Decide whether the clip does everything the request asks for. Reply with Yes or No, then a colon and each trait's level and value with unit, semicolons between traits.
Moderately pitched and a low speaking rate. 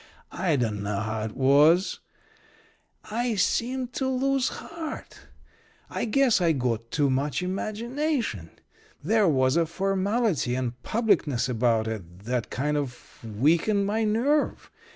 Yes: medium, 165 Hz; slow, 125 wpm